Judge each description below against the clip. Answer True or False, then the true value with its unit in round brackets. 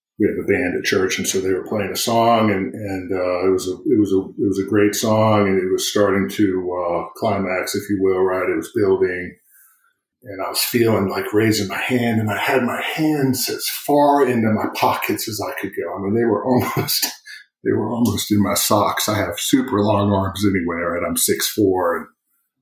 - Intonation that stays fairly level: False (3.4 semitones)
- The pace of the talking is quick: True (225 wpm)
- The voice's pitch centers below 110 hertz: True (100 Hz)